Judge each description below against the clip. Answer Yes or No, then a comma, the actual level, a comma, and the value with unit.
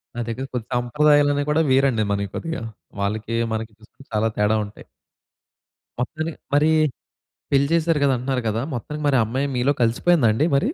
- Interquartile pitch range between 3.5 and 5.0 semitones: Yes, average, 4.7 semitones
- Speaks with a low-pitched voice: Yes, low, 130 Hz